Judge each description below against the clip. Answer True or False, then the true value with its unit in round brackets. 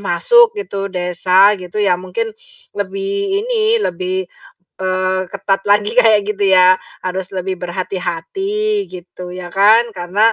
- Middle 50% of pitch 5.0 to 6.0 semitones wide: True (5.5 semitones)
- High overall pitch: True (195 Hz)